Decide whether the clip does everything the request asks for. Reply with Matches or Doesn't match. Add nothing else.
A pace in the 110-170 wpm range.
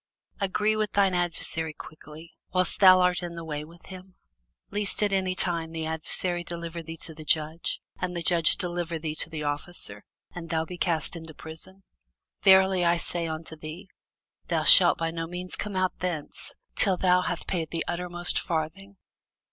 Doesn't match